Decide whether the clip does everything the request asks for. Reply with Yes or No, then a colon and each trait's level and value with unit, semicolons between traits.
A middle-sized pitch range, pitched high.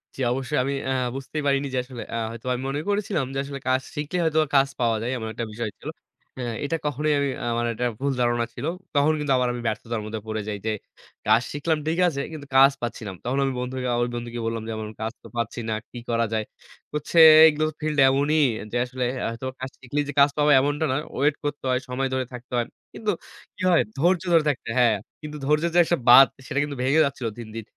No: average, 3.7 semitones; low, 135 Hz